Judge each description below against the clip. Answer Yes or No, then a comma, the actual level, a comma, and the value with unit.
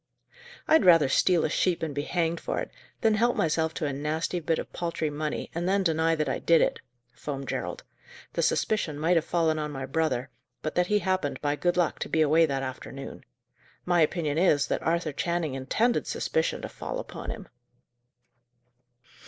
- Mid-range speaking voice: Yes, medium, 160 Hz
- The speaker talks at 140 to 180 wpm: No, average, 190 wpm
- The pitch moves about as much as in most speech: Yes, average, 3.1 semitones